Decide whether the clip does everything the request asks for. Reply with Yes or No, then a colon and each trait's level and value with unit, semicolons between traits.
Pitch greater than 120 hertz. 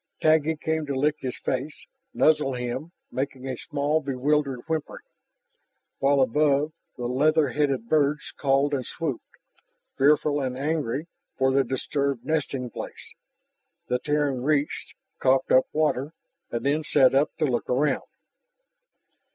Yes: medium, 140 Hz